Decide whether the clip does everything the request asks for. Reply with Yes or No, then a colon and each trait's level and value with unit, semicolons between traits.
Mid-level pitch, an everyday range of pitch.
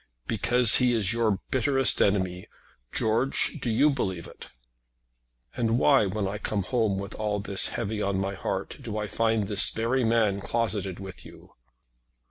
No: low, 110 Hz; average, 3.0 semitones